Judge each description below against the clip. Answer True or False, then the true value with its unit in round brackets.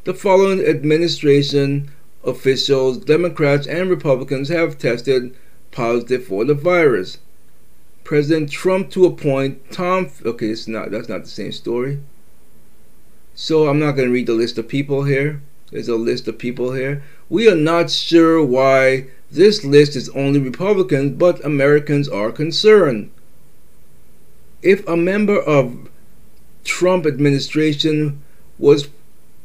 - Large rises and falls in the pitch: False (3.8 semitones)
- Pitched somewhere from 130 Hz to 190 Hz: True (140 Hz)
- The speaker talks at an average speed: False (130 wpm)